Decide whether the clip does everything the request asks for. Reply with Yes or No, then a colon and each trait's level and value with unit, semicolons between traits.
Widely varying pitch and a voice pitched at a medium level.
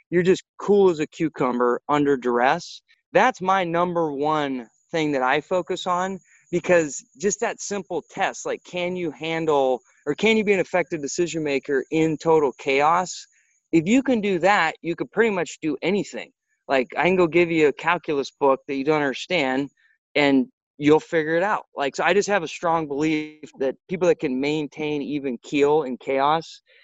No: average, 4.1 semitones; medium, 160 Hz